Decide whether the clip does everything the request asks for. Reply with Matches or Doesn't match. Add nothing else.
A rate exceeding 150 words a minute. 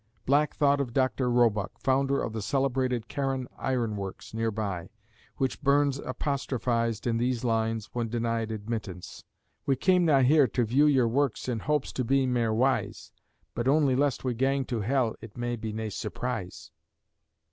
Matches